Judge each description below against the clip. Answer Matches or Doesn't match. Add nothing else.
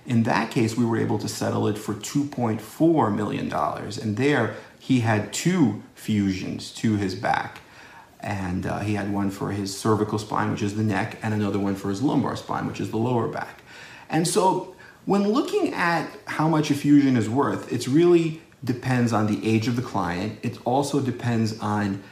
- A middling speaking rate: Matches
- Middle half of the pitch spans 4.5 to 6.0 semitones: Matches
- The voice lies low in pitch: Matches